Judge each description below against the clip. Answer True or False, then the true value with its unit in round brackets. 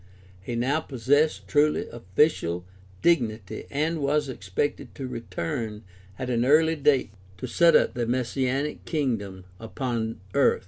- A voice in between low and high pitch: False (130 Hz)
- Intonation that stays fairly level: False (4.6 semitones)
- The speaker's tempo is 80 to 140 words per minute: True (135 wpm)